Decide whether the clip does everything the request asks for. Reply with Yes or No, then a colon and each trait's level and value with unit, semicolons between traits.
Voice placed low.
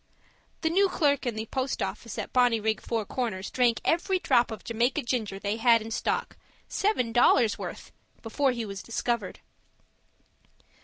No: high, 235 Hz